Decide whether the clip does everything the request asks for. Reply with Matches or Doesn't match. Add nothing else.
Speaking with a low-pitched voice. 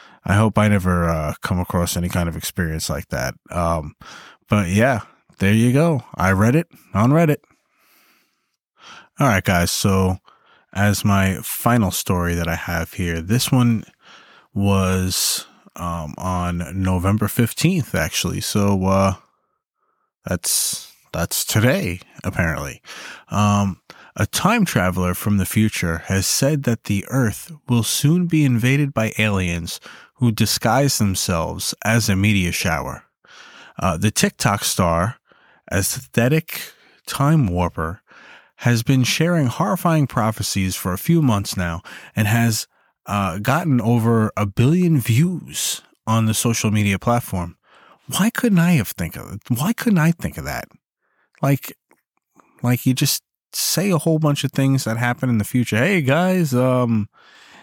Matches